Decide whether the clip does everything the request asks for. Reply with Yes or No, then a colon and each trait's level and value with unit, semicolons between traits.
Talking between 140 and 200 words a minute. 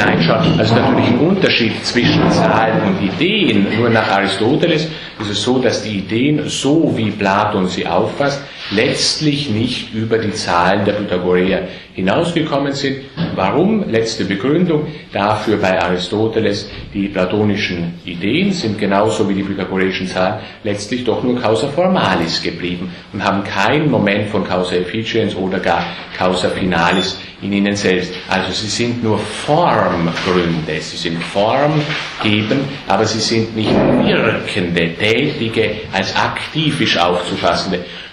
No: average, 130 wpm